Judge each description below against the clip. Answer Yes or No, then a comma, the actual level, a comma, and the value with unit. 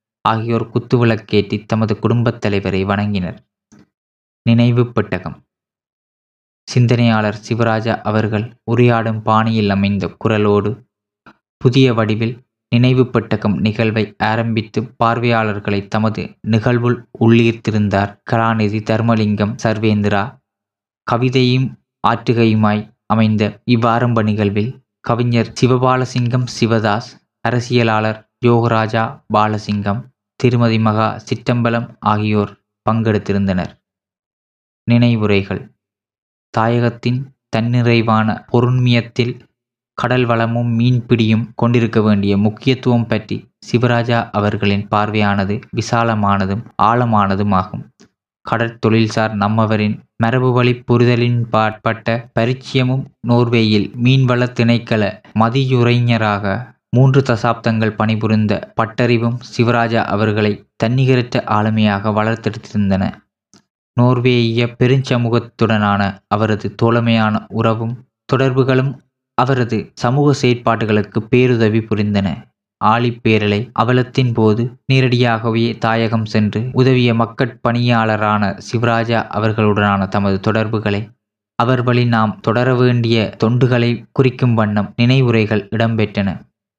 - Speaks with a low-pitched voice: Yes, low, 115 Hz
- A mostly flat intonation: Yes, narrow, 2.3 semitones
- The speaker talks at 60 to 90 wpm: Yes, slow, 75 wpm